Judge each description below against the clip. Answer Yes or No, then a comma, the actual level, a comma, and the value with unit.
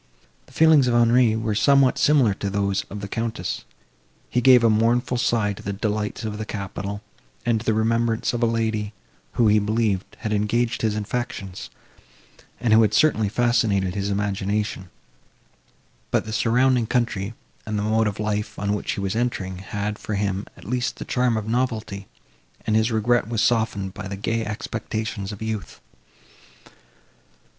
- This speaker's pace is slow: No, average, 170 wpm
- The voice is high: No, low, 110 Hz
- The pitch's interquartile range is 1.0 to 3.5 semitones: Yes, narrow, 2.4 semitones